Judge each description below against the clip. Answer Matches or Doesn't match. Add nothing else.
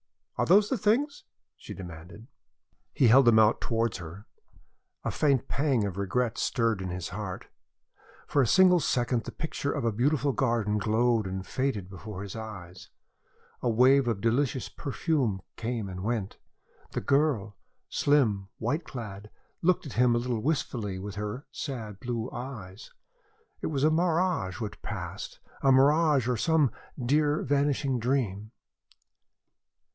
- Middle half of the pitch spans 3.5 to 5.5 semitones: Matches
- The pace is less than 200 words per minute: Matches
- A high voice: Doesn't match